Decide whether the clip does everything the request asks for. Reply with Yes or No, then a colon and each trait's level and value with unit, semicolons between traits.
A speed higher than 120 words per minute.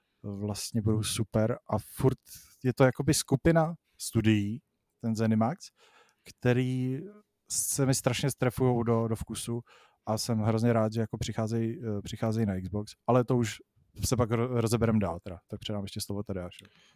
Yes: average, 150 wpm